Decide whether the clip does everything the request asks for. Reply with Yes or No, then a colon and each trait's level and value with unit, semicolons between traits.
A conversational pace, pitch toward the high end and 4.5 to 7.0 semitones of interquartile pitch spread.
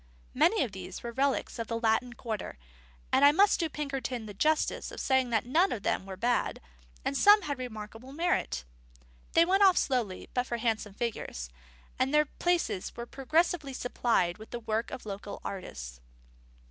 Yes: average, 175 wpm; high, 245 Hz; wide, 5.4 semitones